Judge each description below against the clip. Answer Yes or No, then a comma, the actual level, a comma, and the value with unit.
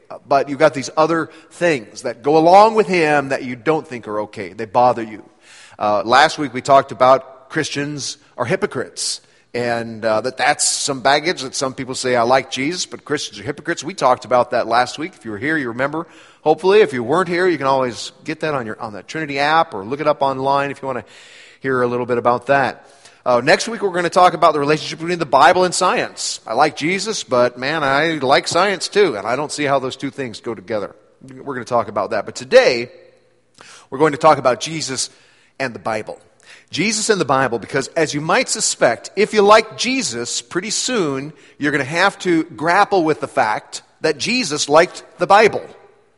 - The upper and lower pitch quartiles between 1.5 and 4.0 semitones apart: No, average, 4.8 semitones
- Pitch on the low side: No, medium, 150 Hz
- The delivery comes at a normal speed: No, fast, 220 wpm